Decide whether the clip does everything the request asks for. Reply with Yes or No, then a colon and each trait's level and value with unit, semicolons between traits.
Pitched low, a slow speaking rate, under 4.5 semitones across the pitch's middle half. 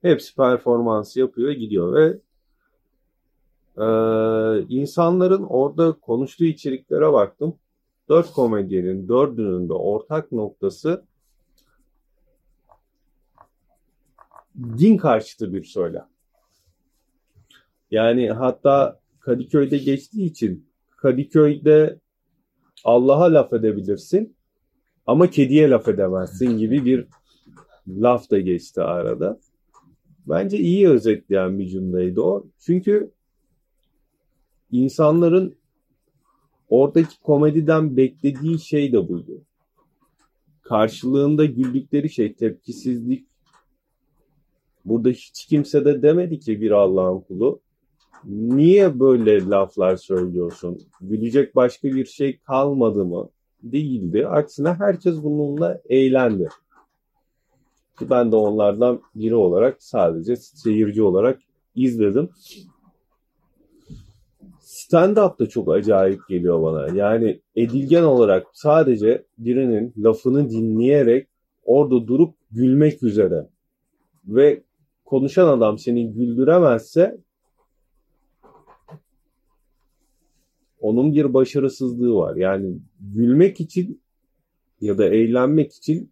No: low, 130 Hz; slow, 85 wpm; wide, 5.6 semitones